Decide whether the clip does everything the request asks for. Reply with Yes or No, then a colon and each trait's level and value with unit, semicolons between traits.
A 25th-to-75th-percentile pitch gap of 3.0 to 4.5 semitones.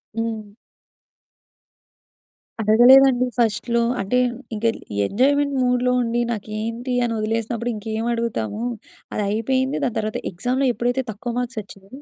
No: narrow, 2.5 semitones